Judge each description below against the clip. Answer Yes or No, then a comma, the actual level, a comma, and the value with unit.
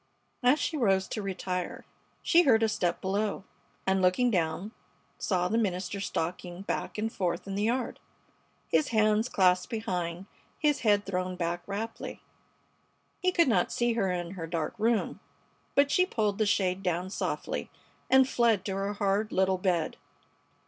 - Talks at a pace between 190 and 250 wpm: No, average, 160 wpm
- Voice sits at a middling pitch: No, high, 195 Hz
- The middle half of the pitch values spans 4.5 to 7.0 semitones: No, average, 3.7 semitones